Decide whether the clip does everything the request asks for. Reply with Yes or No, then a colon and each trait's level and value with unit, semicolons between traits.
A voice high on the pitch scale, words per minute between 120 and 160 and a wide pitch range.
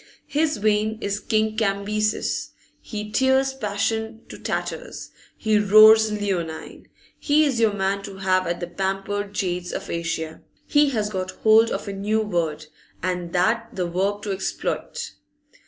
No: high, 205 Hz; average, 150 wpm; average, 2.7 semitones